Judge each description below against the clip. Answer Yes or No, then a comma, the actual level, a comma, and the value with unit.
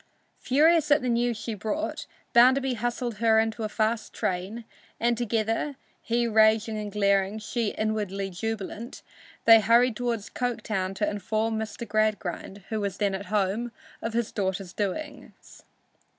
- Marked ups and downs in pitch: No, narrow, 2.4 semitones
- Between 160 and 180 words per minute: No, average, 150 wpm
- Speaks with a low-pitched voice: No, high, 220 Hz